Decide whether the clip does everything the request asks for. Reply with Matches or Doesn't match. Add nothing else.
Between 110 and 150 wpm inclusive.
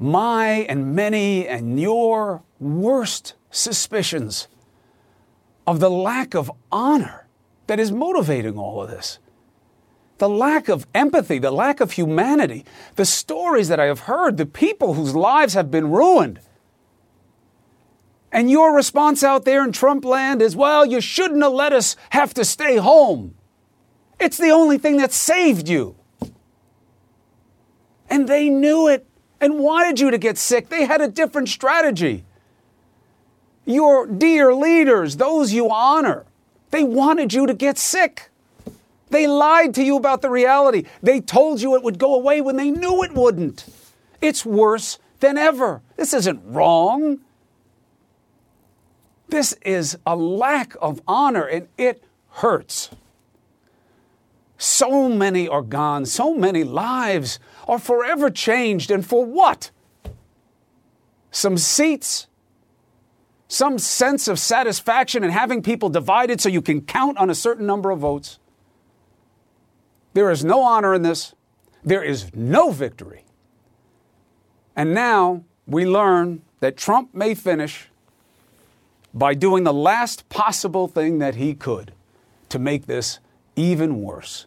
Matches